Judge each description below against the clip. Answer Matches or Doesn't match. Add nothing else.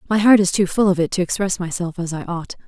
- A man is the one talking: Doesn't match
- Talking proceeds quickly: Matches